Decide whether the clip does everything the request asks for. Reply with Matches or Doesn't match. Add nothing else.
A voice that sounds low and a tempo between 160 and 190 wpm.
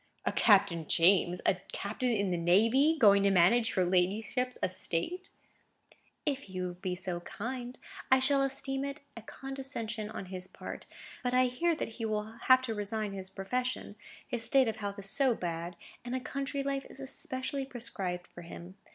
Doesn't match